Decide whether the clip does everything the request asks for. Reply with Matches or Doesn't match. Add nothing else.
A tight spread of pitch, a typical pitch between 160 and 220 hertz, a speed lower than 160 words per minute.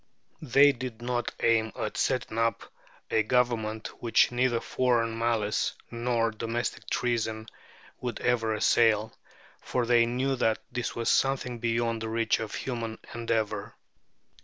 Doesn't match